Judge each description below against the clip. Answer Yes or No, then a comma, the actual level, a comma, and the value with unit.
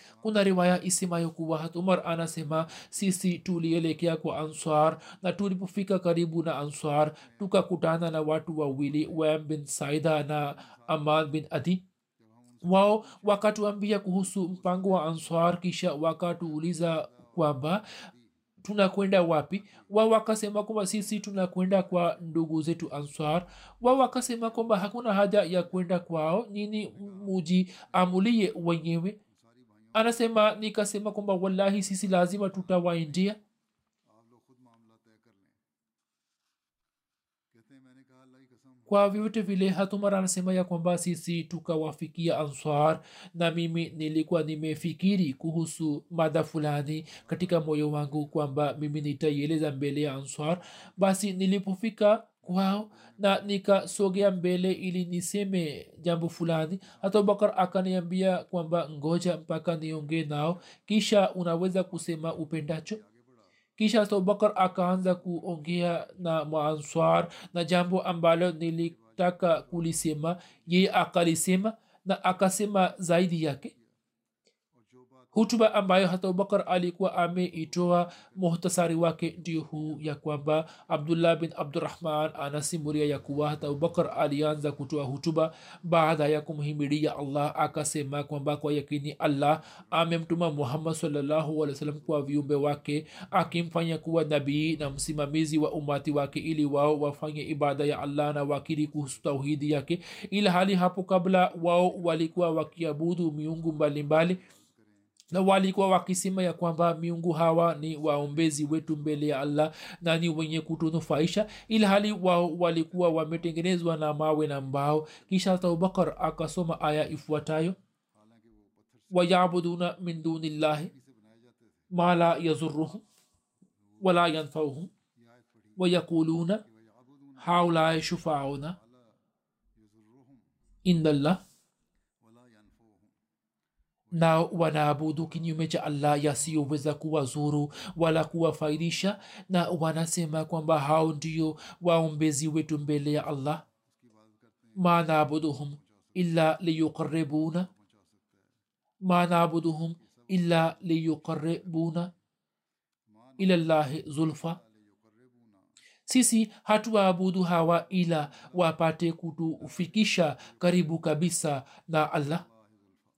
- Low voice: No, medium, 165 Hz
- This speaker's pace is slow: Yes, slow, 85 wpm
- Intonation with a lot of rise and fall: No, average, 3.2 semitones